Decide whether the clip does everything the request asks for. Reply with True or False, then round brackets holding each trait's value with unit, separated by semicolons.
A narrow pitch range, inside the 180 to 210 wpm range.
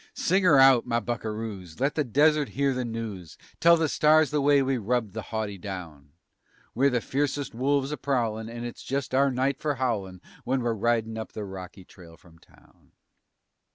False (4.6 semitones; 190 wpm)